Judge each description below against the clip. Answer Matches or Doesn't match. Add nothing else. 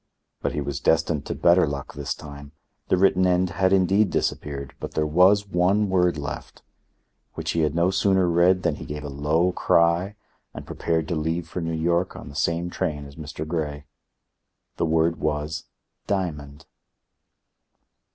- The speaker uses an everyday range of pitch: Matches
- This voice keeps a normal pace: Matches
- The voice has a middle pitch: Doesn't match